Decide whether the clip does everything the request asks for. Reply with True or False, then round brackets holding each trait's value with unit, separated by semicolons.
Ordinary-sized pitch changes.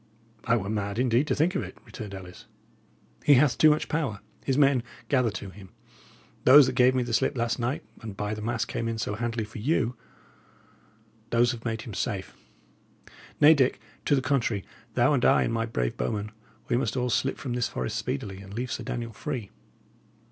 True (3.5 semitones)